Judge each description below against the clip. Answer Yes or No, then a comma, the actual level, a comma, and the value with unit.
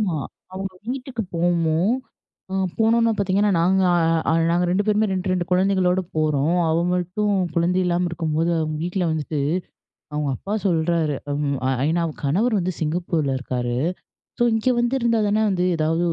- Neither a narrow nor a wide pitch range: Yes, average, 4.1 semitones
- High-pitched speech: No, medium, 180 Hz